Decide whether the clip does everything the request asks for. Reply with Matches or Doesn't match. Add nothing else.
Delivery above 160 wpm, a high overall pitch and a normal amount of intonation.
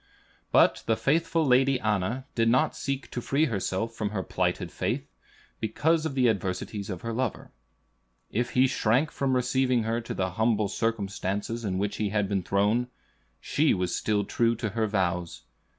Doesn't match